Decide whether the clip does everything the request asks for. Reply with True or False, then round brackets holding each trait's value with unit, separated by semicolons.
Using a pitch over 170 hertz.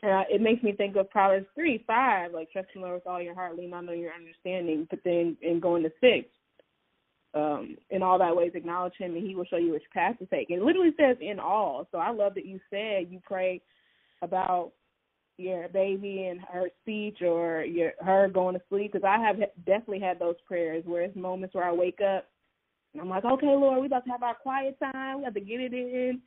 True (185 Hz)